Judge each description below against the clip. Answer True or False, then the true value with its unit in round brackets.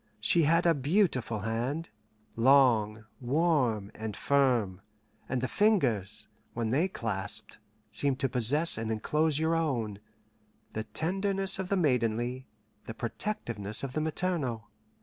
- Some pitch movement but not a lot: False (6.3 semitones)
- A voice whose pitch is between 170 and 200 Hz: False (130 Hz)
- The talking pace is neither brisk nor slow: False (130 wpm)